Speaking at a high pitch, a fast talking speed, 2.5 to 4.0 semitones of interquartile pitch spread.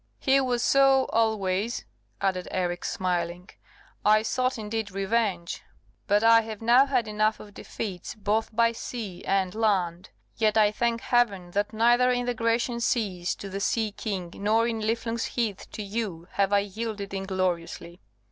No: high, 215 Hz; average, 155 wpm; average, 3.1 semitones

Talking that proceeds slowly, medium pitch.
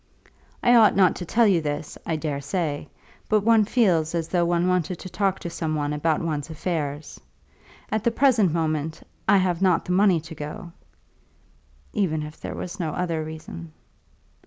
No: average, 180 wpm; medium, 170 Hz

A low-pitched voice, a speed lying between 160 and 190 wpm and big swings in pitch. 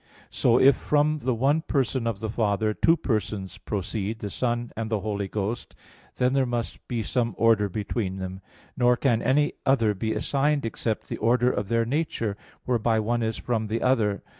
No: low, 115 Hz; average, 180 wpm; average, 3.1 semitones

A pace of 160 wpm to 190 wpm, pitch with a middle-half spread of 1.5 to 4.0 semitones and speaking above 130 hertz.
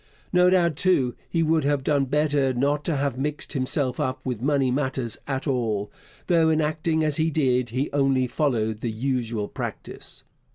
Yes: average, 175 wpm; average, 3.3 semitones; medium, 140 Hz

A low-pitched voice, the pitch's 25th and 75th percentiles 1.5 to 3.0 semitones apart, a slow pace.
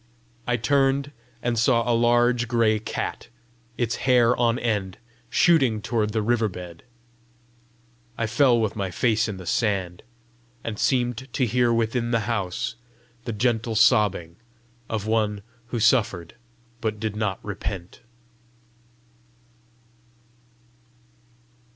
Yes: low, 115 Hz; narrow, 2.4 semitones; slow, 120 wpm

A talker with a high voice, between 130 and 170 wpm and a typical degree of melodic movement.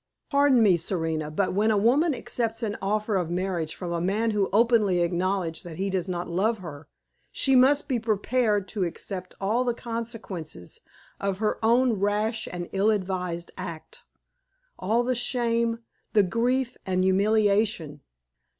Yes: high, 205 Hz; average, 155 wpm; average, 4.0 semitones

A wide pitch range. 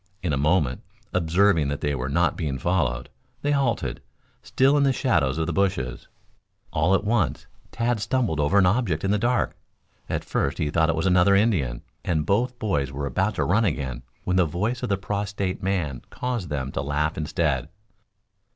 Yes: wide, 5.8 semitones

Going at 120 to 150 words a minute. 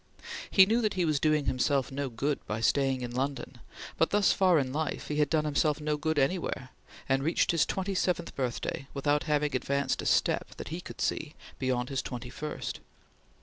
No: average, 195 wpm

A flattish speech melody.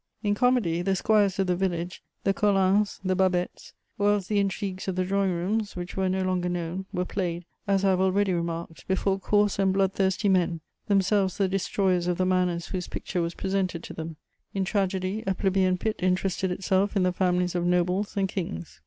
Yes: narrow, 1.6 semitones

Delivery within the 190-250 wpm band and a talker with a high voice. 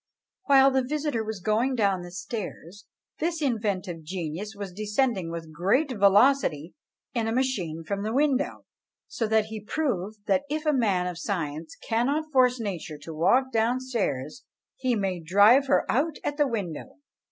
No: average, 160 wpm; high, 220 Hz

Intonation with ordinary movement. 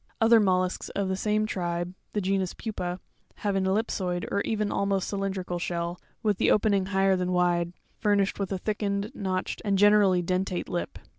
No: narrow, 2.1 semitones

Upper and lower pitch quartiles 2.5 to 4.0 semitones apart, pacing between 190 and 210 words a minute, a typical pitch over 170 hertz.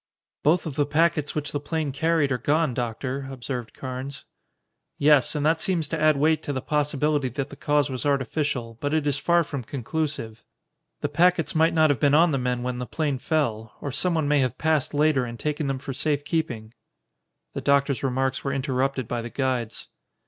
No: average, 3.0 semitones; average, 195 wpm; medium, 145 Hz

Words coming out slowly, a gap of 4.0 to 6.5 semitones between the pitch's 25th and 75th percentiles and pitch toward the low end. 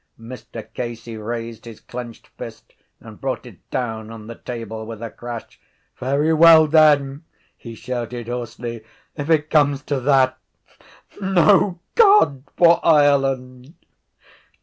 Yes: slow, 125 wpm; average, 4.3 semitones; low, 130 Hz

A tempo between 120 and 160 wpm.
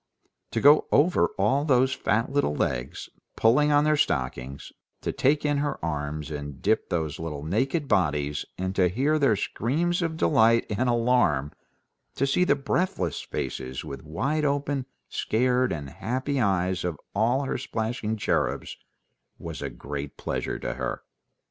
Yes: average, 155 wpm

